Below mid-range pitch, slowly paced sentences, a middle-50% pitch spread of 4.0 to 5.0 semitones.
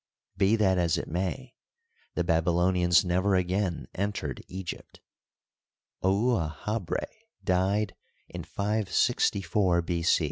No: very low, 95 Hz; slow, 100 wpm; average, 2.7 semitones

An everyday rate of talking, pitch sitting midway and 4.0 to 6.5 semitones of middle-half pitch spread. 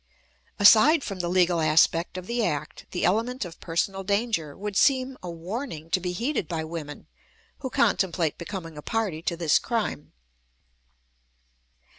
Yes: average, 150 wpm; medium, 180 Hz; average, 5.3 semitones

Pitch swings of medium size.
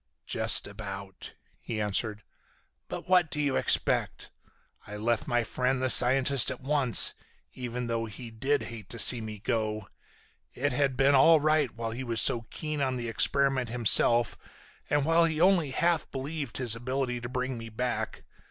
Yes: average, 3.4 semitones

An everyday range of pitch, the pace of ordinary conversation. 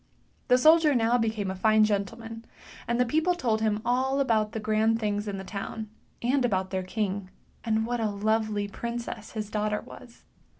No: narrow, 2.2 semitones; average, 180 wpm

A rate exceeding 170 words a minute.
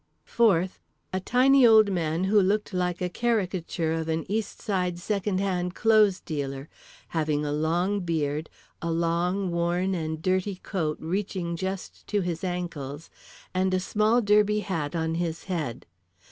No: average, 145 wpm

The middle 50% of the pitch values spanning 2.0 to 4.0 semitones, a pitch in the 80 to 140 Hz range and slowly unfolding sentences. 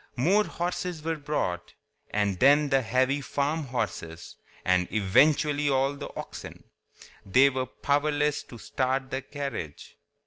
Yes: average, 3.6 semitones; low, 135 Hz; slow, 130 wpm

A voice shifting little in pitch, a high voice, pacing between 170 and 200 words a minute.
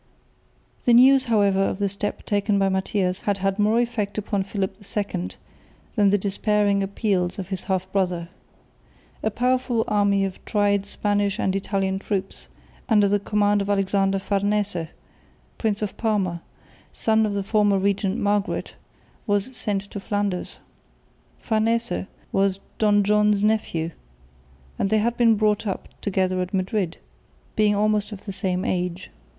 No: narrow, 1.6 semitones; high, 200 Hz; average, 145 wpm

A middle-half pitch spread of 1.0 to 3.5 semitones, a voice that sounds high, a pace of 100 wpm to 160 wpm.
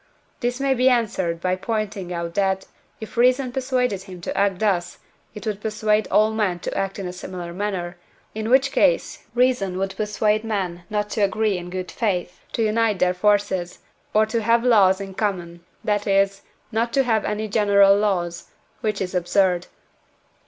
No: average, 2.9 semitones; high, 205 Hz; average, 175 wpm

